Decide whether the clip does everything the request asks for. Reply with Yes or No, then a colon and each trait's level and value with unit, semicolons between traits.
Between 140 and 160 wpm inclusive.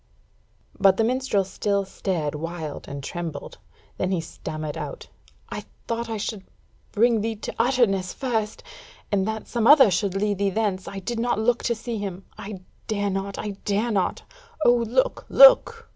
No: average, 170 wpm